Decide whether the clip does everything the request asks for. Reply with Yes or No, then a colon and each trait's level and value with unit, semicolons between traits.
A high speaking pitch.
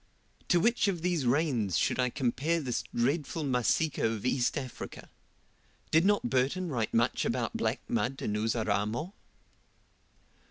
No: low, 130 Hz